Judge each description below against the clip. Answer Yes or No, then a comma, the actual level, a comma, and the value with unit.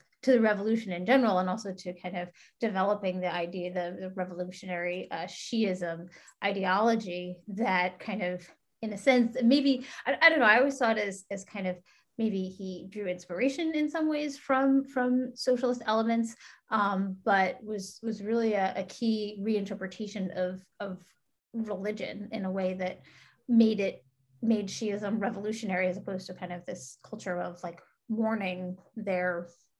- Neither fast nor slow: Yes, average, 165 wpm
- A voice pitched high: Yes, high, 200 Hz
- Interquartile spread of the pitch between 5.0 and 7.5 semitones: No, average, 3.8 semitones